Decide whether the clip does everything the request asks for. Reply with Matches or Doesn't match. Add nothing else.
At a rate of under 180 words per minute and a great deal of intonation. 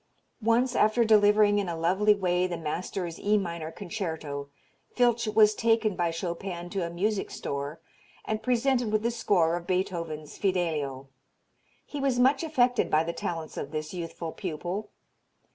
Doesn't match